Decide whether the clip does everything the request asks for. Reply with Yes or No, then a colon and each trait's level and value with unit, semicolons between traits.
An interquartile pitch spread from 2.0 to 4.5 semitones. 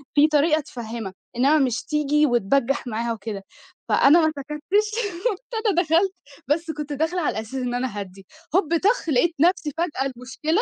No: wide, 5.6 semitones